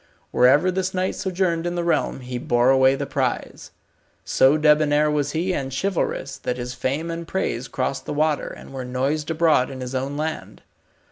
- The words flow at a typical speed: Yes, average, 185 wpm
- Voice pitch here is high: No, medium, 145 Hz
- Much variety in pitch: No, average, 4.1 semitones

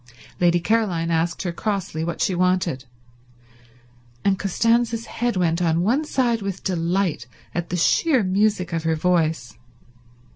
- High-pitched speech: No, medium, 180 Hz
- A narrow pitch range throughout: No, average, 4.2 semitones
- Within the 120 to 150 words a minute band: Yes, average, 140 wpm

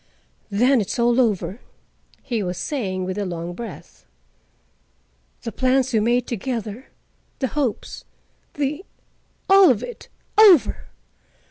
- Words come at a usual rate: No, slow, 110 wpm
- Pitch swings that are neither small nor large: Yes, average, 4.9 semitones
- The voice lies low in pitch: No, high, 235 Hz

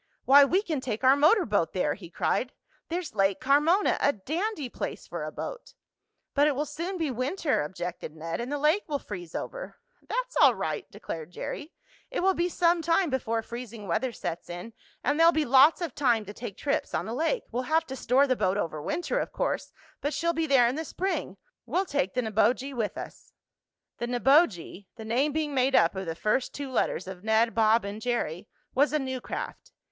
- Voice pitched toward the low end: No, very high, 260 Hz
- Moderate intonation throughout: No, wide, 6.5 semitones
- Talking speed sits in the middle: No, fast, 210 wpm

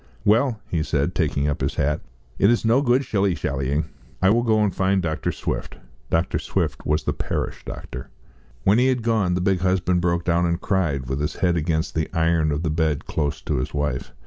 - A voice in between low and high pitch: No, very low, 85 Hz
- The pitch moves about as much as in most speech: Yes, average, 4.7 semitones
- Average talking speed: No, fast, 210 wpm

